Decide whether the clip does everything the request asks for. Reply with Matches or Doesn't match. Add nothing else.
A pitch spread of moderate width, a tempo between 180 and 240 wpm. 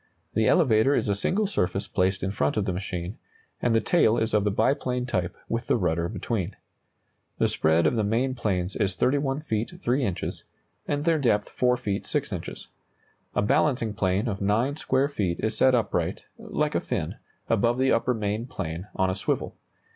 Matches